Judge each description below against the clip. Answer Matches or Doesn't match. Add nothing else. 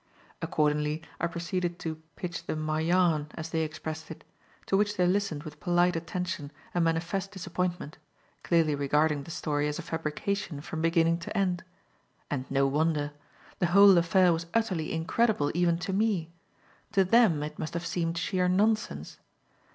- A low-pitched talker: Doesn't match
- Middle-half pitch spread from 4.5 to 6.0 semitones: Doesn't match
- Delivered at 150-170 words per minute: Matches